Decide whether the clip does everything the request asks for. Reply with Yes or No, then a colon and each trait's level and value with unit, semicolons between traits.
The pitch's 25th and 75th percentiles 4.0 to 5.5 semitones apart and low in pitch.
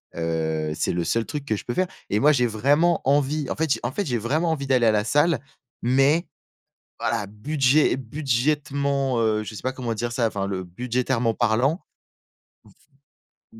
Yes: average, 4.7 semitones; low, 125 Hz